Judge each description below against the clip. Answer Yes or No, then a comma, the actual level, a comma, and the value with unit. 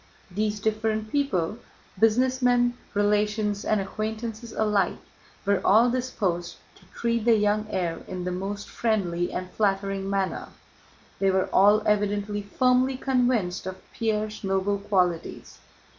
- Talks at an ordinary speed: No, slow, 115 wpm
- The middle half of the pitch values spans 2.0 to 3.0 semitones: Yes, narrow, 2.4 semitones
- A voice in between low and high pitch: No, high, 210 Hz